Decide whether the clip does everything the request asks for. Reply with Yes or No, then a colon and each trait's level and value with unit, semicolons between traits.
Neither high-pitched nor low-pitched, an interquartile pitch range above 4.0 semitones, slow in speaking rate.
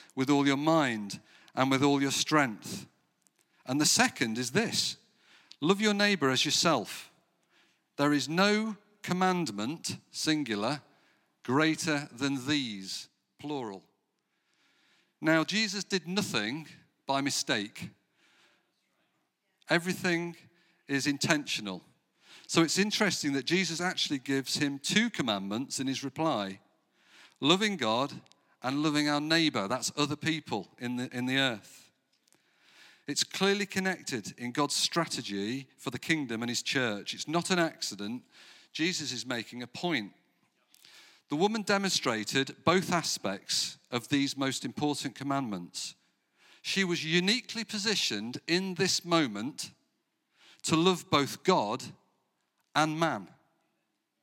Yes: medium, 150 Hz; average, 4.8 semitones; slow, 120 wpm